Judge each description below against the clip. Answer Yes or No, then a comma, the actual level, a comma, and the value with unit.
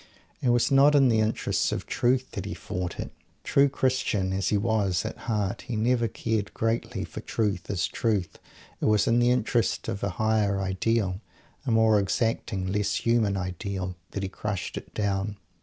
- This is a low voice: Yes, low, 105 Hz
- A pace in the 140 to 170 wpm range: No, average, 180 wpm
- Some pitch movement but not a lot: Yes, average, 3.1 semitones